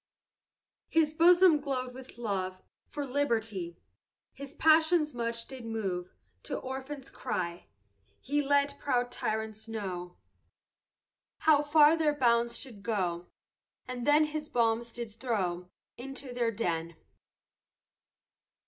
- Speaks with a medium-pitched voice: No, high, 245 Hz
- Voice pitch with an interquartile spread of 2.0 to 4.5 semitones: No, average, 5.0 semitones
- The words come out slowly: Yes, slow, 110 wpm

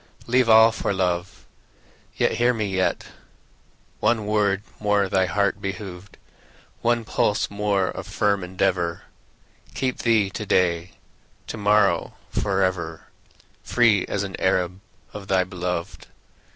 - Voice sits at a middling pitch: No, low, 100 Hz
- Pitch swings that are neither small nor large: No, narrow, 2.3 semitones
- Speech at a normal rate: No, slow, 125 wpm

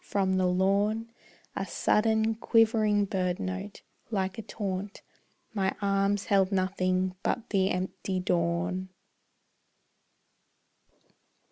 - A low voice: No, high, 195 Hz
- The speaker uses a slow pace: Yes, slow, 95 wpm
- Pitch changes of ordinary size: No, narrow, 1.9 semitones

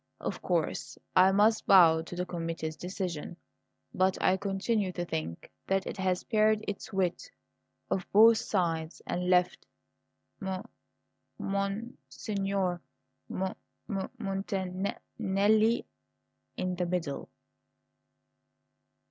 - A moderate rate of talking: No, slow, 115 wpm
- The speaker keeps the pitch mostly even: Yes, narrow, 2.0 semitones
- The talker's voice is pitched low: No, high, 190 Hz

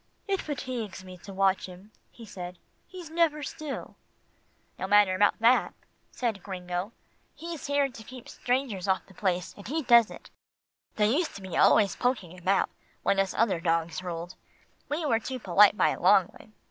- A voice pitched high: Yes, high, 205 Hz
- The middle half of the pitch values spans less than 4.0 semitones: No, wide, 5.6 semitones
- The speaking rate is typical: Yes, average, 175 wpm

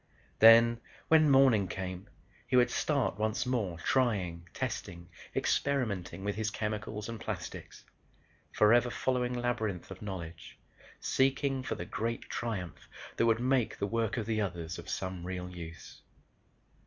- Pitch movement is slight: No, average, 4.8 semitones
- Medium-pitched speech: No, low, 110 Hz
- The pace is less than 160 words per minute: Yes, average, 140 wpm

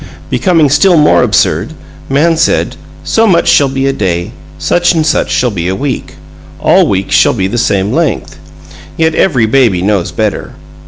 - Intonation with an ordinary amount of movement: No, wide, 8.3 semitones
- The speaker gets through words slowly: No, average, 170 wpm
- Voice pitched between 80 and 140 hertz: Yes, low, 135 Hz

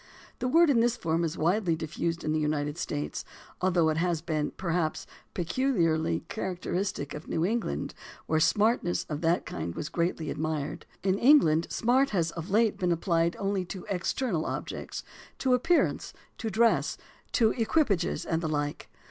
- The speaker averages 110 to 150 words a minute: No, average, 160 wpm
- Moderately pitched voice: Yes, medium, 170 Hz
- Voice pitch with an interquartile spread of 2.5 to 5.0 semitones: No, wide, 5.5 semitones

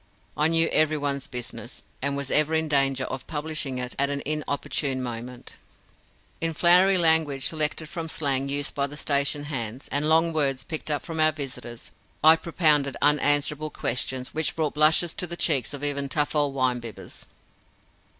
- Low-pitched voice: No, medium, 145 Hz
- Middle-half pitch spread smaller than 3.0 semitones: Yes, narrow, 2.5 semitones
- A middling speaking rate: Yes, average, 170 wpm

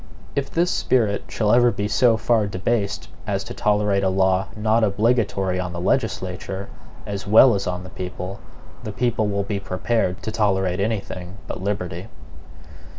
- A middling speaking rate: Yes, average, 165 wpm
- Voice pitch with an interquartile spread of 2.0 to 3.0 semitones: Yes, average, 2.7 semitones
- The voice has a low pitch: Yes, low, 100 Hz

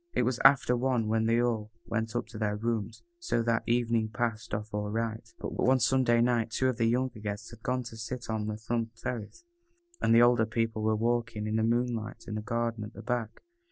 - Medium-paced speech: No, fast, 225 wpm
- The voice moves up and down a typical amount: No, narrow, 1.6 semitones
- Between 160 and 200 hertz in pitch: No, low, 115 Hz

